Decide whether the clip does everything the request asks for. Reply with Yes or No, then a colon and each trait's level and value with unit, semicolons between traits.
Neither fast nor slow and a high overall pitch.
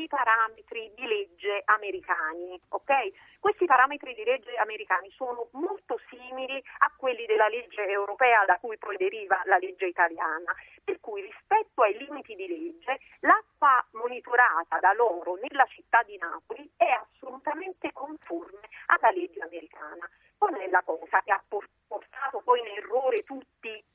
Yes: average, 145 wpm; very high, 260 Hz